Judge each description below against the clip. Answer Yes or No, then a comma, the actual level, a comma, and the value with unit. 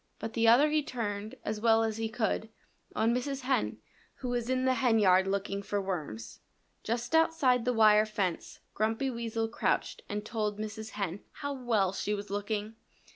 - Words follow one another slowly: No, average, 175 wpm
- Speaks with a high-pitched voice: Yes, high, 220 Hz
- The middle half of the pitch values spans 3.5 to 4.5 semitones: No, average, 3.0 semitones